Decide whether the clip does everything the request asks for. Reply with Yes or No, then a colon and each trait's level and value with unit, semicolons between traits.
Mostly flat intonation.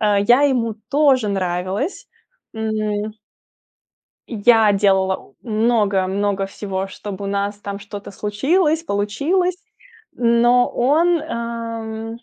No: average, 3.3 semitones